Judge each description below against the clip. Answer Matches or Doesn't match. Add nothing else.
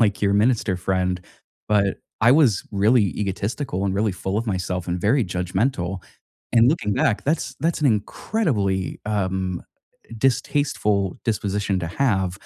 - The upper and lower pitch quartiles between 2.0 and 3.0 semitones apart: Doesn't match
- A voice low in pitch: Matches